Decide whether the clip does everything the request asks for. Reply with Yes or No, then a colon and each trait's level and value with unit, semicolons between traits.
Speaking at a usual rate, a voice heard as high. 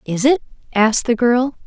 Yes: average, 180 wpm; high, 240 Hz